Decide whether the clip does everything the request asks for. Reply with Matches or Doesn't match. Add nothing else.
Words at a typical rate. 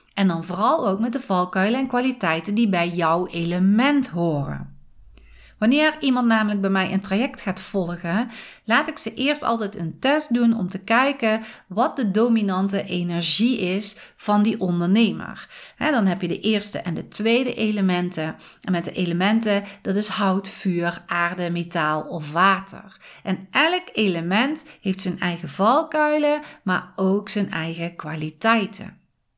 Matches